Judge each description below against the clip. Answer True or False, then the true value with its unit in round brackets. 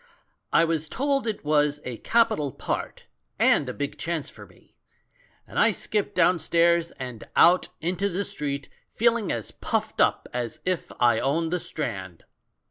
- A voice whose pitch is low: False (160 Hz)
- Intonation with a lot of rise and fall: False (4.7 semitones)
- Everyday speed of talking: True (160 wpm)